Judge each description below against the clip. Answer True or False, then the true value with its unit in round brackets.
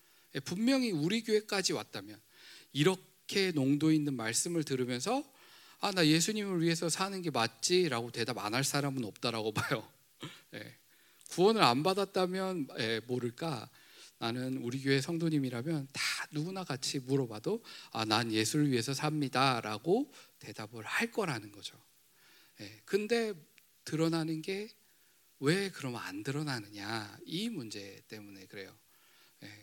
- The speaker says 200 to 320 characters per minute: True (275 characters per minute)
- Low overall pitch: False (145 Hz)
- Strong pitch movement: True (7.9 semitones)